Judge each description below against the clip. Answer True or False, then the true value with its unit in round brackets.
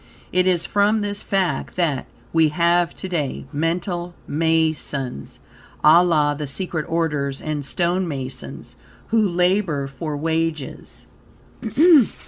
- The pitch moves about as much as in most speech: True (3.3 semitones)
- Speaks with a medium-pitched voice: True (165 Hz)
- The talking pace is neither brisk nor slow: False (115 wpm)